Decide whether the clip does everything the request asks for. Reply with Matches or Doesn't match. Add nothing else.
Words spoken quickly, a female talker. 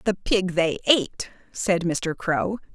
Doesn't match